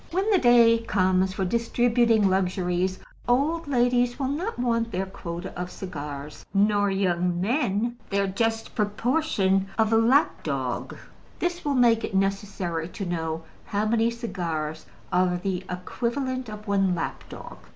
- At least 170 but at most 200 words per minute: No, average, 140 wpm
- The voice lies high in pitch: Yes, high, 205 Hz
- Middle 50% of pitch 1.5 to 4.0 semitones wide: No, average, 4.6 semitones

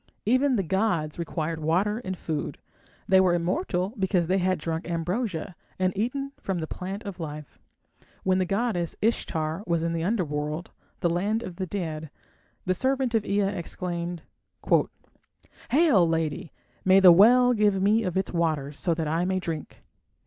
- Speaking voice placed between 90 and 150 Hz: No, medium, 185 Hz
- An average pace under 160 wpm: No, average, 165 wpm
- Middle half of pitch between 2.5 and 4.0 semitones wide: Yes, average, 3.7 semitones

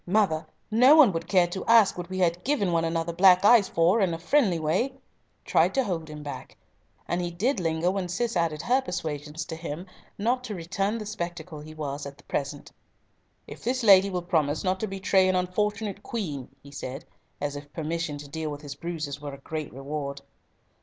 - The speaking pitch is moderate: Yes, medium, 175 Hz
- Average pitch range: Yes, average, 4.5 semitones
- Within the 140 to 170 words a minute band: No, average, 200 wpm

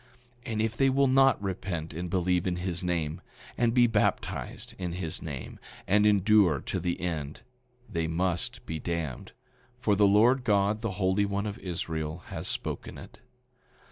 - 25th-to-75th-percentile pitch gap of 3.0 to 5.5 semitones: Yes, average, 3.9 semitones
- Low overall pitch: Yes, very low, 95 Hz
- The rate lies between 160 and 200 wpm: Yes, average, 170 wpm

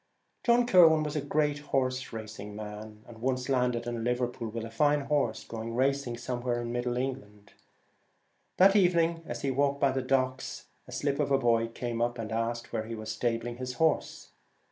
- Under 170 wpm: No, average, 190 wpm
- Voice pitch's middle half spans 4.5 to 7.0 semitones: No, average, 3.4 semitones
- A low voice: Yes, low, 125 Hz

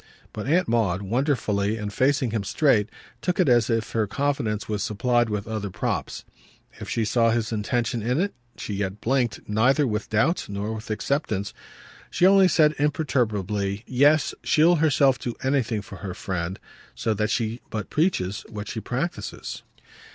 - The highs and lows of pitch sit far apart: No, average, 4.8 semitones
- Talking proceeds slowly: No, average, 165 wpm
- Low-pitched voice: Yes, low, 115 Hz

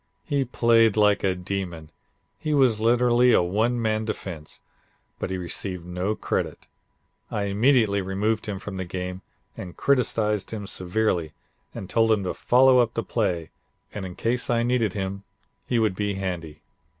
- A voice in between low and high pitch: No, low, 105 Hz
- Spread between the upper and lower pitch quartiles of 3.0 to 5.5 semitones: Yes, average, 3.8 semitones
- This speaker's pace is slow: No, average, 160 wpm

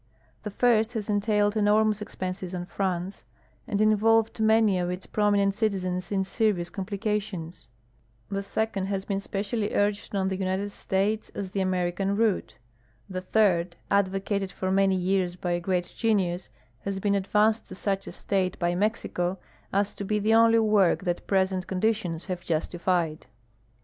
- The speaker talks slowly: No, average, 165 wpm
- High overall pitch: Yes, high, 195 Hz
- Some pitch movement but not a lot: No, narrow, 2.3 semitones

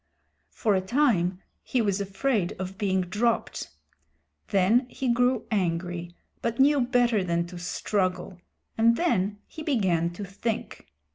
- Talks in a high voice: Yes, high, 200 Hz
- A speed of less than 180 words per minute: Yes, slow, 135 wpm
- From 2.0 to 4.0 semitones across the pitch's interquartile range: No, average, 4.7 semitones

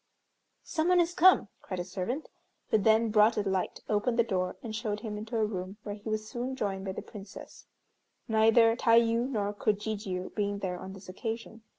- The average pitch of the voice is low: No, high, 215 Hz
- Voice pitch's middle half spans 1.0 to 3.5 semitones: Yes, narrow, 2.5 semitones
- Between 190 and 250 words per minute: Yes, average, 195 wpm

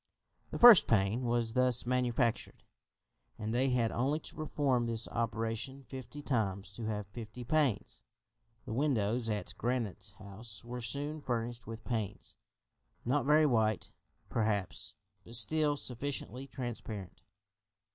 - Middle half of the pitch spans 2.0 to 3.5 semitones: Yes, average, 3.1 semitones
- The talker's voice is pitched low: Yes, low, 120 Hz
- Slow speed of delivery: Yes, slow, 125 wpm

